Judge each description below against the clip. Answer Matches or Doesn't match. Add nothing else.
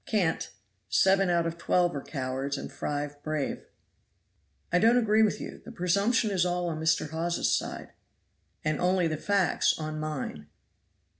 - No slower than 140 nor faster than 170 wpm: Matches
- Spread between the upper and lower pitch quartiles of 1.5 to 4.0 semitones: Matches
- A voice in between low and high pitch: Matches